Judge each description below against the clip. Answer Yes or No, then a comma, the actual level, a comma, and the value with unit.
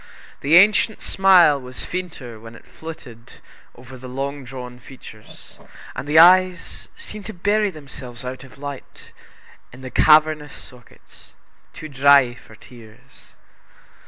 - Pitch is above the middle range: No, medium, 140 Hz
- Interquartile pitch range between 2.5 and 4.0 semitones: No, average, 4.7 semitones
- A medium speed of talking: No, slow, 130 wpm